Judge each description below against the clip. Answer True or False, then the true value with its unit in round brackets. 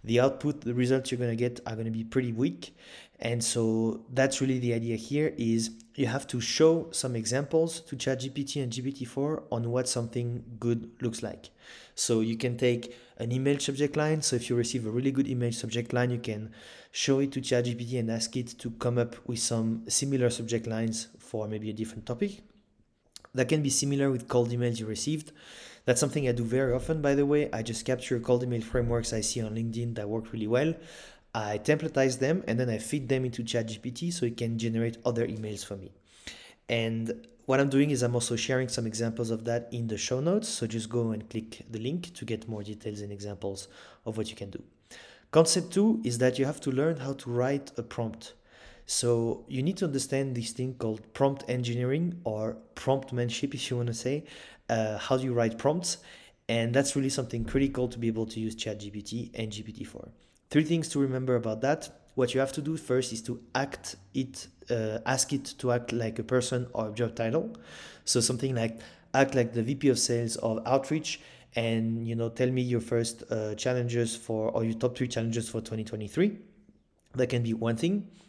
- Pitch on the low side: True (120 Hz)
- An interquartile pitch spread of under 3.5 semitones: True (3.0 semitones)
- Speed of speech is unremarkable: False (210 wpm)